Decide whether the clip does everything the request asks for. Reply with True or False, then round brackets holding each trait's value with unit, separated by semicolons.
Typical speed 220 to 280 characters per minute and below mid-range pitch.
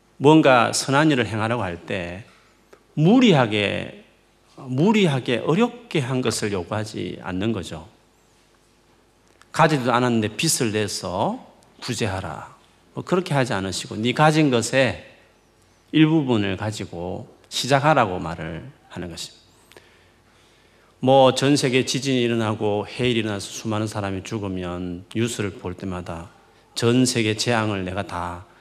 True (265 characters per minute; 110 Hz)